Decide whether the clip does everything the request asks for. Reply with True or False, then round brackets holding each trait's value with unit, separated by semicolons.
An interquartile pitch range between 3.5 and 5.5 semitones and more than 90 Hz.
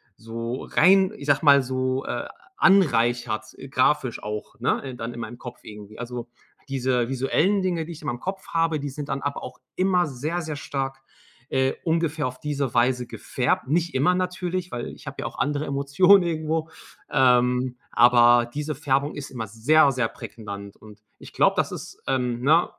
True (4.4 semitones; 135 Hz)